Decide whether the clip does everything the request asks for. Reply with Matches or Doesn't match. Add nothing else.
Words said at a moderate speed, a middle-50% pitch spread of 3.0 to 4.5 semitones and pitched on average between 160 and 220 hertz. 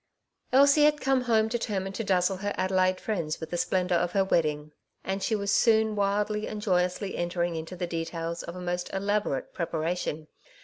Matches